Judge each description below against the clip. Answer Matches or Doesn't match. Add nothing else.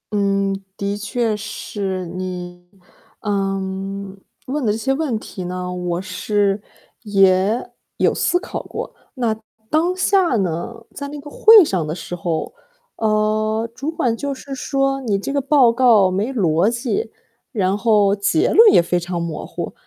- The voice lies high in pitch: Matches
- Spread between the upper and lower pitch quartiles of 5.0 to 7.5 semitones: Matches